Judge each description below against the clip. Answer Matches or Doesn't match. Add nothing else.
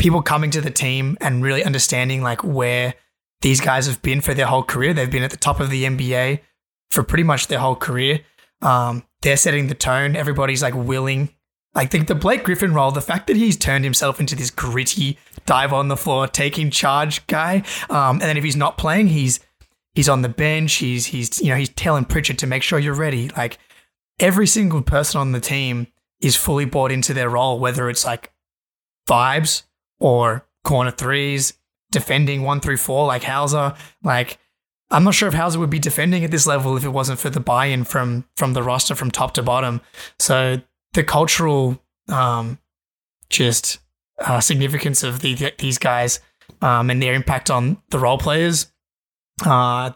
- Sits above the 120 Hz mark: Matches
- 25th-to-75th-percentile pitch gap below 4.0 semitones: Matches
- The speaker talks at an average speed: Matches